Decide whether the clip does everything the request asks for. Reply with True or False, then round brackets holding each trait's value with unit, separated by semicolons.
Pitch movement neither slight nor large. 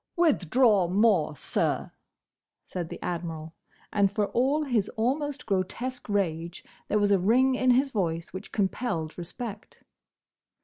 False (6.1 semitones)